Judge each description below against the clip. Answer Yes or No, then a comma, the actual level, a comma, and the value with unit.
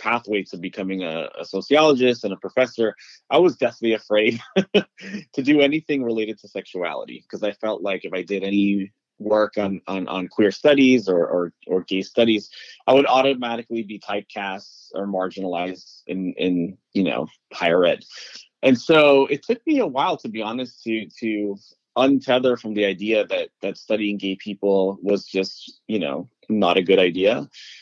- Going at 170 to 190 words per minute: Yes, average, 175 wpm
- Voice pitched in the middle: No, low, 110 Hz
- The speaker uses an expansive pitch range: Yes, wide, 5.7 semitones